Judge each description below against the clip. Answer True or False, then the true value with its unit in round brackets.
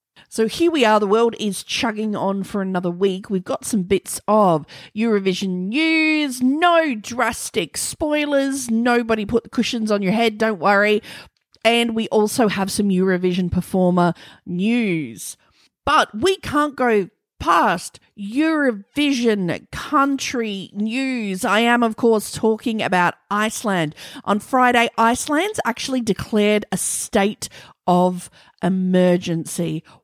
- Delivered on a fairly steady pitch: False (4.1 semitones)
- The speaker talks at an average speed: False (125 wpm)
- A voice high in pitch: True (215 Hz)